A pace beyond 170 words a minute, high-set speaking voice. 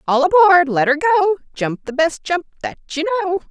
Yes: fast, 205 wpm; very high, 320 Hz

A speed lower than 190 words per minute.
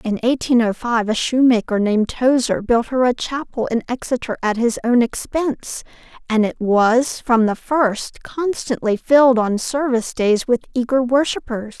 Yes: average, 165 wpm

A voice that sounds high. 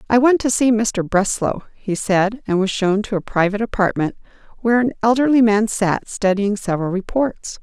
Yes: high, 210 Hz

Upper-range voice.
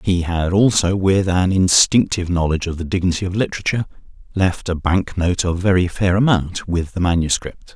No: very low, 90 Hz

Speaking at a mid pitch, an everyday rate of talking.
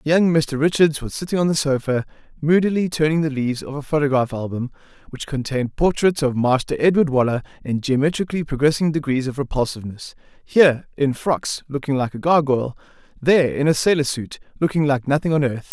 Yes: medium, 145 Hz; average, 170 wpm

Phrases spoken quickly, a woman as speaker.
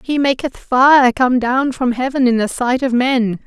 Yes: fast, 210 wpm; female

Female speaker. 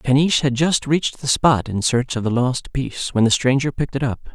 No: male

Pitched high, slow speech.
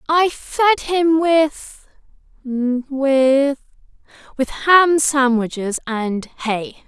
Yes: very high, 280 Hz; slow, 70 wpm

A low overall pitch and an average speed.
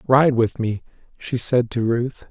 Yes: low, 120 Hz; average, 180 wpm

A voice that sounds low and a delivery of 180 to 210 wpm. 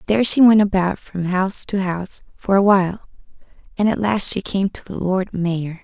No: high, 190 Hz; fast, 205 wpm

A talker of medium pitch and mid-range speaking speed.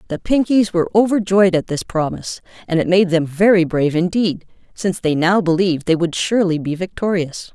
Yes: medium, 180 Hz; average, 185 wpm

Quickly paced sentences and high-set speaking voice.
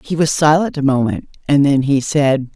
No: fast, 210 wpm; medium, 140 Hz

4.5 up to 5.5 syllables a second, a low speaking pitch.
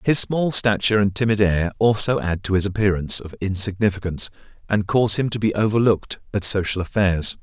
No: 6.0 syllables/s; low, 100 Hz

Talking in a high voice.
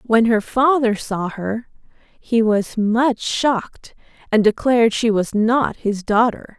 Yes: high, 225 Hz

